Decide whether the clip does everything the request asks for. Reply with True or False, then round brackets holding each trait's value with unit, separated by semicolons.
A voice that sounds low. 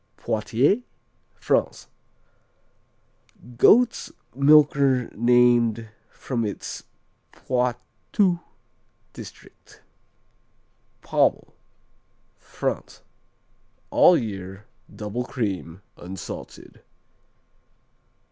True (120 Hz)